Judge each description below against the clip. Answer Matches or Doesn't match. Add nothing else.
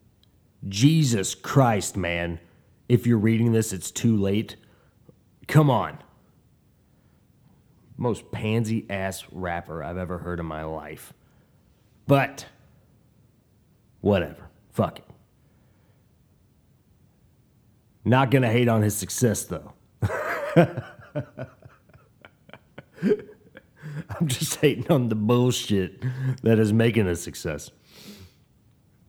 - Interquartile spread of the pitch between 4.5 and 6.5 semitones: Matches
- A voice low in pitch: Matches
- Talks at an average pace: Doesn't match